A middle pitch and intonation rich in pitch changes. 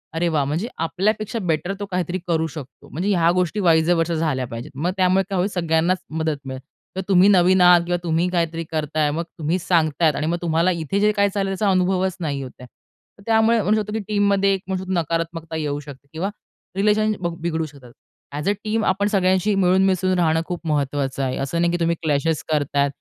No: medium, 170 Hz; average, 3.3 semitones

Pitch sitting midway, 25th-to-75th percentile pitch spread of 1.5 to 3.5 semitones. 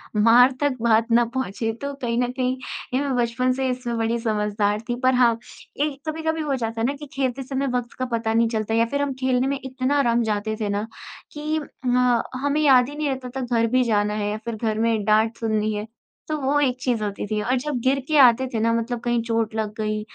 No: high, 240 Hz; average, 3.0 semitones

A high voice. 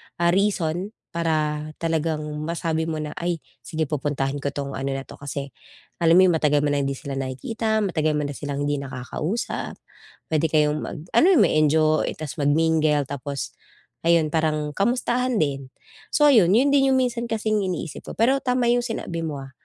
No: medium, 160 Hz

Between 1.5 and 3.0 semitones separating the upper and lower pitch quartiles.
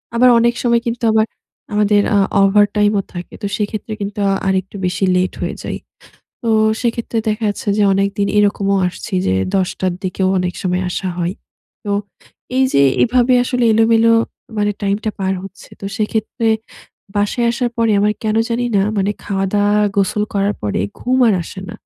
Yes: average, 2.7 semitones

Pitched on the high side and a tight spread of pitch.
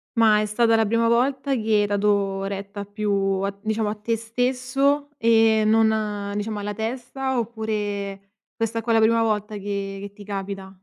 Yes: high, 215 Hz; narrow, 2.1 semitones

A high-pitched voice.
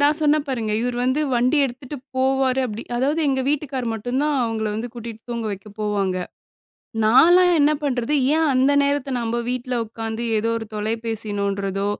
Yes: high, 245 Hz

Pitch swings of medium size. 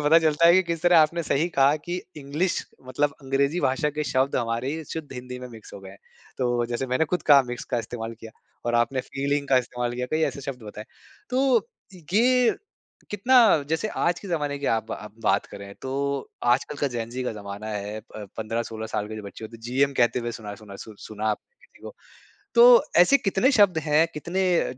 No: wide, 5.8 semitones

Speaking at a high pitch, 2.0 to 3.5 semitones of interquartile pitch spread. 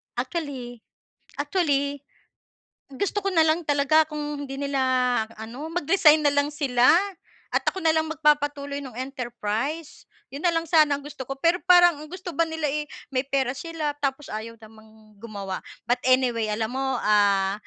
No: very high, 280 Hz; average, 4.2 semitones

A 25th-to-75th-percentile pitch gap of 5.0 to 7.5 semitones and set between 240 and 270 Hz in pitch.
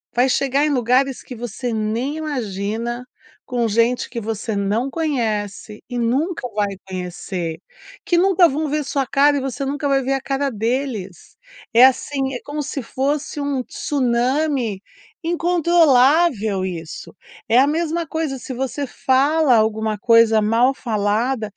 No: average, 4.4 semitones; very high, 255 Hz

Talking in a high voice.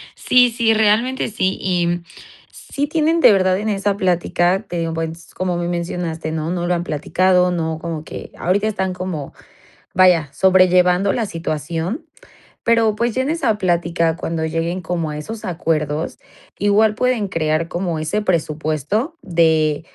No: medium, 180 Hz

